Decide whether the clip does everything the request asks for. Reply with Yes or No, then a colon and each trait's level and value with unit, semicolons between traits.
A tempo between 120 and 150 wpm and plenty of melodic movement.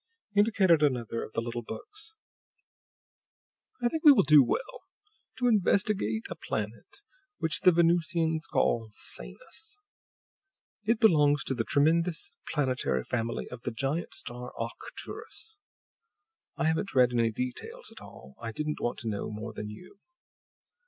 Yes: average, 140 wpm; wide, 7.7 semitones